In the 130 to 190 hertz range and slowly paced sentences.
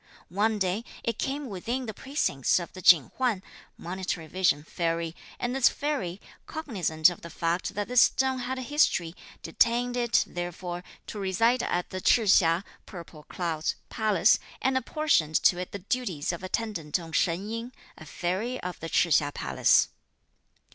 No: medium, 185 Hz; average, 165 wpm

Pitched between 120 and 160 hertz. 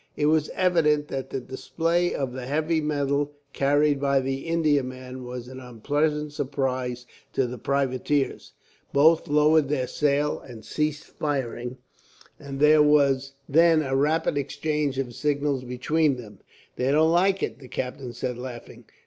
Yes: medium, 140 Hz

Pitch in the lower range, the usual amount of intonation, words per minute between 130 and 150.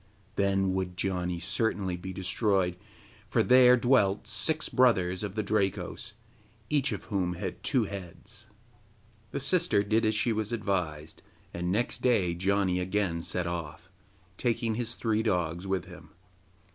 Yes: low, 100 Hz; average, 3.7 semitones; average, 145 wpm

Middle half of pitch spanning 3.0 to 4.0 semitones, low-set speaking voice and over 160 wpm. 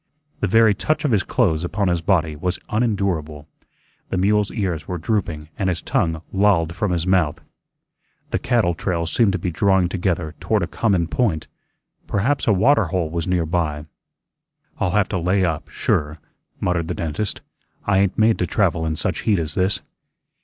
Yes: average, 3.7 semitones; very low, 90 Hz; average, 180 wpm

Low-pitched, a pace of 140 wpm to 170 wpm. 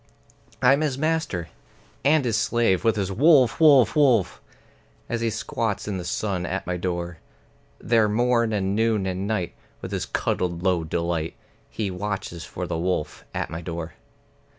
Yes: low, 100 Hz; average, 160 wpm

